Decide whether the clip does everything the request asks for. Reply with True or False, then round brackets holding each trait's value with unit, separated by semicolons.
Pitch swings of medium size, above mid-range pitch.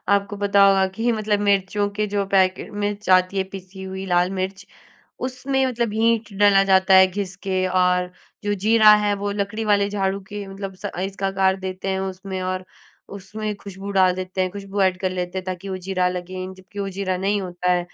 False (1.6 semitones; 195 Hz)